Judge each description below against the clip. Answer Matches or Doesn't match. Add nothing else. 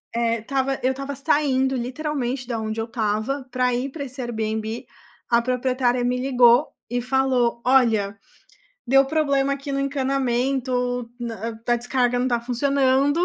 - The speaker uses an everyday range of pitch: Doesn't match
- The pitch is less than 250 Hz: Doesn't match